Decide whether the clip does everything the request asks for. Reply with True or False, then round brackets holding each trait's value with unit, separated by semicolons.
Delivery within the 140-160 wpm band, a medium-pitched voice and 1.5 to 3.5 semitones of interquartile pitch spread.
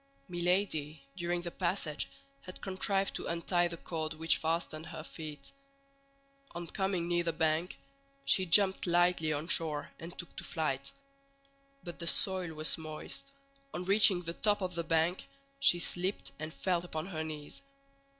True (155 wpm; 170 Hz; 2.4 semitones)